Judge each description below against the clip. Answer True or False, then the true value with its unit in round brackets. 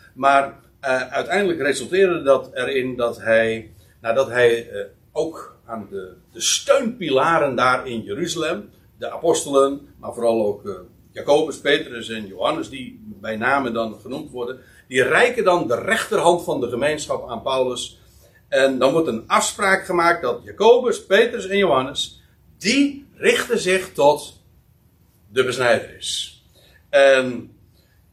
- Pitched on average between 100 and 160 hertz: True (135 Hz)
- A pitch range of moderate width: False (8.6 semitones)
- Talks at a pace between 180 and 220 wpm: False (140 wpm)